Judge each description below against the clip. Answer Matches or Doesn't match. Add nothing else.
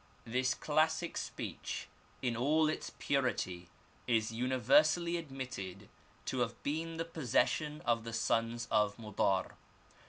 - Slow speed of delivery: Matches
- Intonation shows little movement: Doesn't match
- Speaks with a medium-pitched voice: Doesn't match